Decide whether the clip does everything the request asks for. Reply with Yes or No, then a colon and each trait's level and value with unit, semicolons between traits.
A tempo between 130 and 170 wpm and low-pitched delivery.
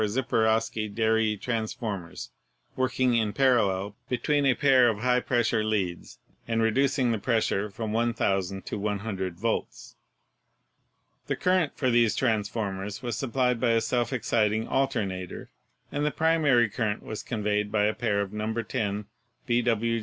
Yes: average, 145 wpm; low, 110 Hz